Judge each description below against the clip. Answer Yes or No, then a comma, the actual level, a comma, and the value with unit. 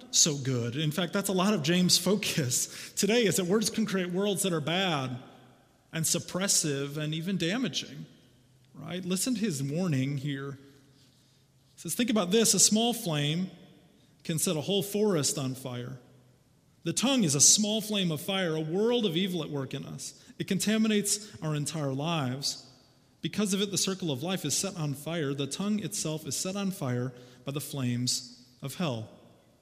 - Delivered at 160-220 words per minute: Yes, average, 180 wpm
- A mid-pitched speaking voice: Yes, medium, 160 Hz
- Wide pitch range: Yes, wide, 6.0 semitones